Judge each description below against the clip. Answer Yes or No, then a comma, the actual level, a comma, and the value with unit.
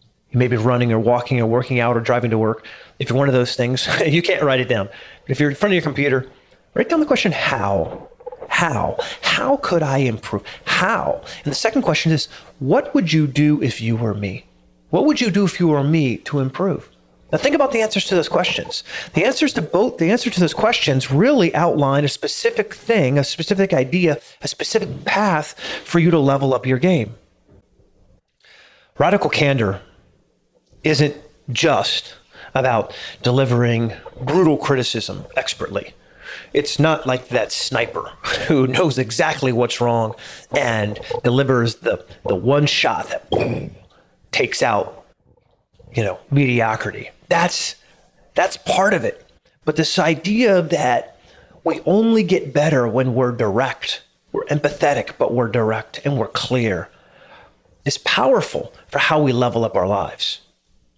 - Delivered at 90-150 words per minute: No, average, 160 wpm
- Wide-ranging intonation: Yes, wide, 5.8 semitones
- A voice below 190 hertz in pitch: Yes, medium, 140 Hz